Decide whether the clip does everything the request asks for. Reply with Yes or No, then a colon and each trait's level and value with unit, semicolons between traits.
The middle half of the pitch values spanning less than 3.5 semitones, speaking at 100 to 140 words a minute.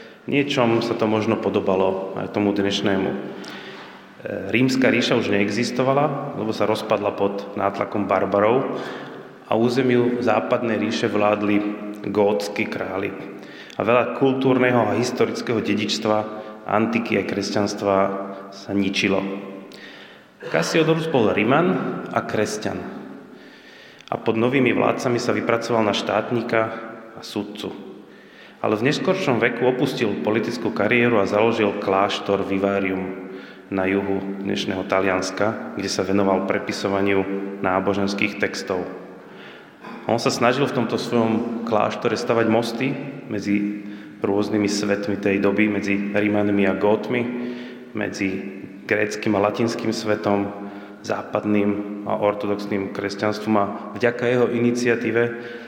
Yes: average, 2.8 semitones; slow, 110 wpm